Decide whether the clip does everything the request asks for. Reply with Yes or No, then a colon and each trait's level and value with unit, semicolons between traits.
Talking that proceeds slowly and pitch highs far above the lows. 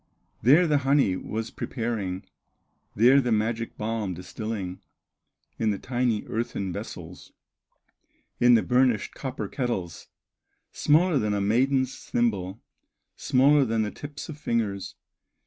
No: slow, 120 wpm; average, 4.1 semitones